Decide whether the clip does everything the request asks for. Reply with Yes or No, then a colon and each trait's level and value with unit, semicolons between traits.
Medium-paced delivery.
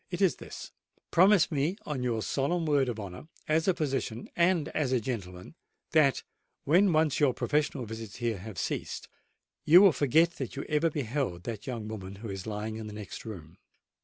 Yes: average, 185 wpm